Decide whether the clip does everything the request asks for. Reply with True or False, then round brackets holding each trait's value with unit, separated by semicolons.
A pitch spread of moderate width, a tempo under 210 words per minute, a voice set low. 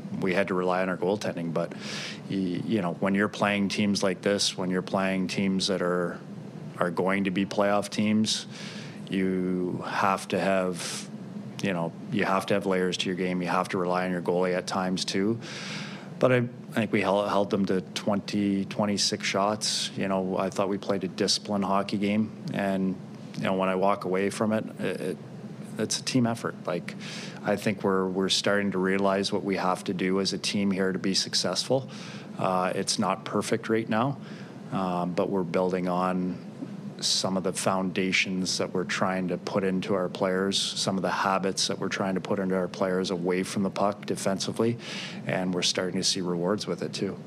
False (1.6 semitones; 200 wpm; 95 Hz)